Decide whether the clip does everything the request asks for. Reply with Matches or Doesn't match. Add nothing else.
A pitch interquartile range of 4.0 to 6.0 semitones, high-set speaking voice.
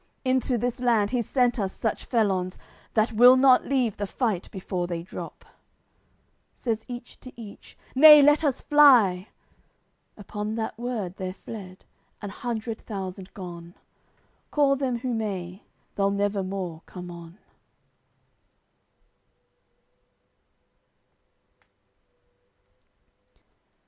Matches